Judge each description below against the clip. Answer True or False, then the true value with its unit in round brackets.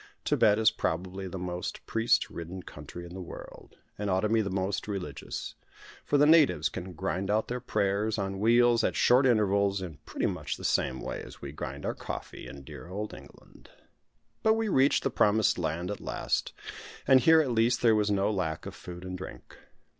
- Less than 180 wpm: False (200 wpm)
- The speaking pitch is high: False (100 Hz)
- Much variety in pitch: False (3.8 semitones)